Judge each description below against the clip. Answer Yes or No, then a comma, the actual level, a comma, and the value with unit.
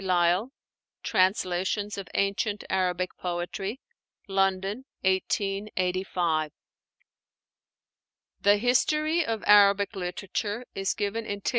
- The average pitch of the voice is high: Yes, high, 195 Hz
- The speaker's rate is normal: No, slow, 90 wpm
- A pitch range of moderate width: No, narrow, 2.2 semitones